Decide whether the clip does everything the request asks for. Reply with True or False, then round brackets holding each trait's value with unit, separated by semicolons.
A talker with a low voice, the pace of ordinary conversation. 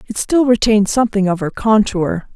False (210 Hz; 180 wpm)